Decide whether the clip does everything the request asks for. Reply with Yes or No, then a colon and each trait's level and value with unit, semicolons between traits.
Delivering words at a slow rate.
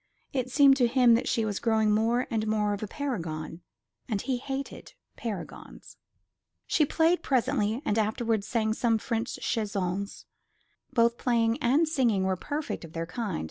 No: average, 160 wpm